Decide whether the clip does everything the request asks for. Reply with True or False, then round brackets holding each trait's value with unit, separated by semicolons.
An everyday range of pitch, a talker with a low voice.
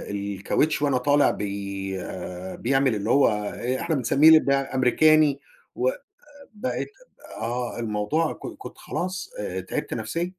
False (6.6 semitones; 130 Hz)